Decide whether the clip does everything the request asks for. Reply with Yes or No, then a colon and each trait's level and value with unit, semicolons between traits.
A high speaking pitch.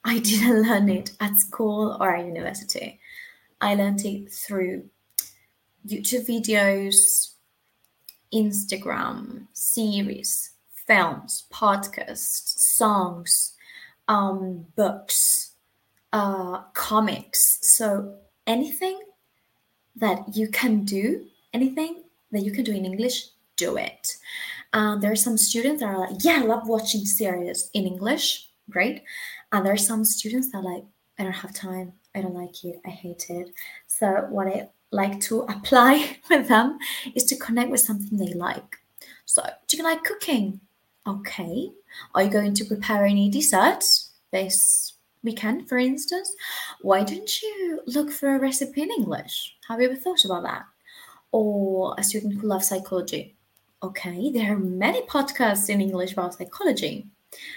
Yes: high, 215 Hz